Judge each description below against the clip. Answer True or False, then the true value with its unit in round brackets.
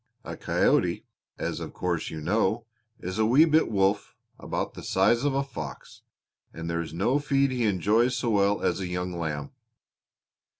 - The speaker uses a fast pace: False (175 wpm)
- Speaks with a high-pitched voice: False (100 Hz)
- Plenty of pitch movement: True (6.0 semitones)